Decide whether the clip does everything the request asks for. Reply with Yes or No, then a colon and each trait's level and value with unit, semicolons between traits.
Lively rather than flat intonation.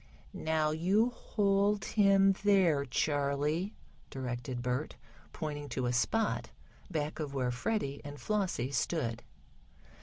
Yes: wide, 6.2 semitones